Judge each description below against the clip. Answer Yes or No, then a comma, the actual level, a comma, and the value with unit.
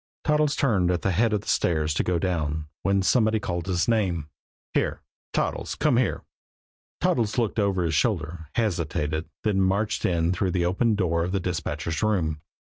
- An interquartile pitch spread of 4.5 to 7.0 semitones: No, average, 4.1 semitones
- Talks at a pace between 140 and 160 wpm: No, average, 175 wpm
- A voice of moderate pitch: No, very low, 90 Hz